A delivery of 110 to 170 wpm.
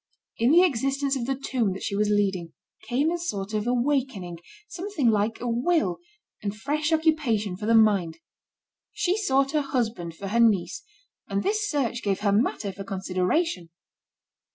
Yes: average, 165 wpm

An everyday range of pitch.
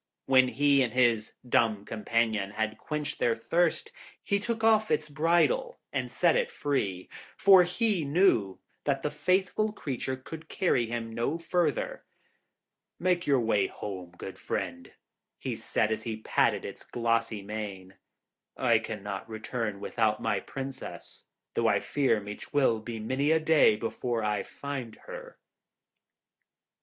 No: wide, 6.7 semitones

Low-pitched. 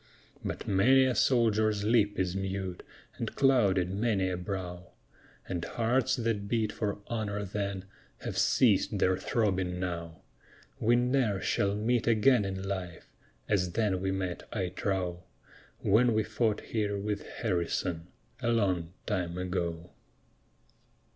Yes: low, 100 Hz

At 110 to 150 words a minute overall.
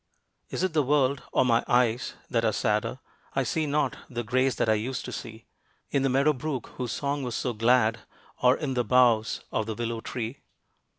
No: average, 200 wpm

